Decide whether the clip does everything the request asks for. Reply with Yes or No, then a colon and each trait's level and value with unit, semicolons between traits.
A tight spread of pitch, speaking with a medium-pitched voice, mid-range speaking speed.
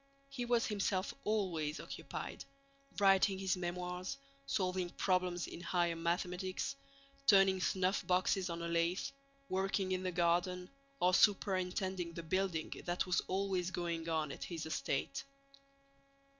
No: narrow, 1.8 semitones; medium, 180 Hz; slow, 125 wpm